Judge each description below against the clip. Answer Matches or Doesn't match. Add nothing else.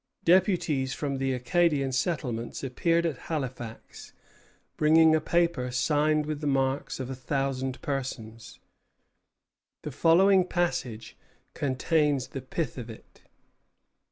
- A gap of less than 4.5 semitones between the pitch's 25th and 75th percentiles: Matches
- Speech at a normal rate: Doesn't match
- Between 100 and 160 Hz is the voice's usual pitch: Matches